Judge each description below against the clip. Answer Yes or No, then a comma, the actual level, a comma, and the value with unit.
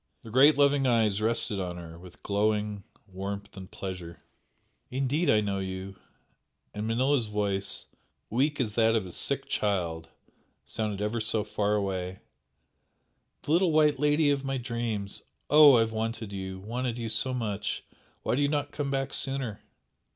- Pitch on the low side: Yes, low, 110 Hz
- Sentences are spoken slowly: No, average, 160 wpm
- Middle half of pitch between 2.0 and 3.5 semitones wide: No, average, 4.9 semitones